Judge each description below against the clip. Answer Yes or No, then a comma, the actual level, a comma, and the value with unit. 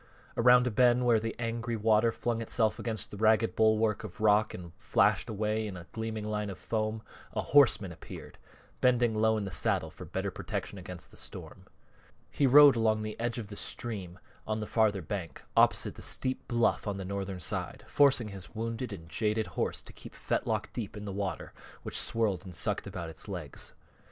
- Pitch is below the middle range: Yes, low, 110 Hz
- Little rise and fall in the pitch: Yes, narrow, 2.3 semitones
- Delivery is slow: No, average, 195 wpm